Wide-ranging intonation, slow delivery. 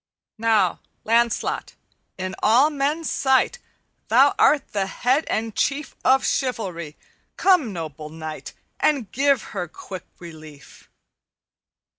Yes: wide, 7.7 semitones; slow, 110 wpm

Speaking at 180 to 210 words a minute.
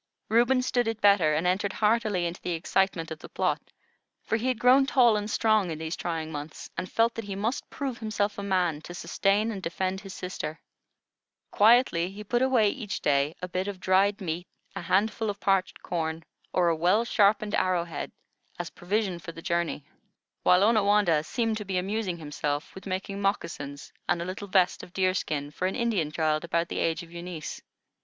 Yes: average, 195 wpm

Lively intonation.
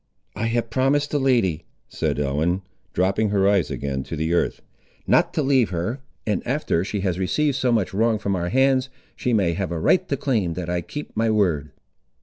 Yes: wide, 6.5 semitones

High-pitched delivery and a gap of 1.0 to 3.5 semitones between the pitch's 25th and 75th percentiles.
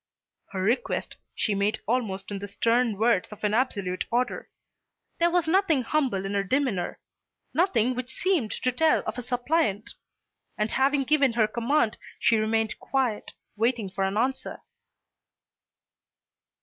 No: high, 235 Hz; average, 4.3 semitones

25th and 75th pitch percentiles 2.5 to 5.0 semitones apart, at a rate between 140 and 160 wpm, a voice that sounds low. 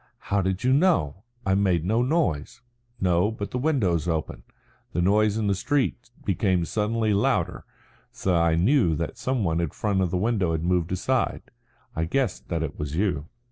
No: average, 4.7 semitones; average, 180 wpm; very low, 95 Hz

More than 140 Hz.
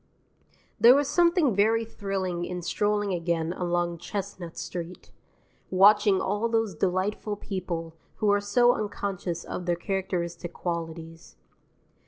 Yes: high, 190 Hz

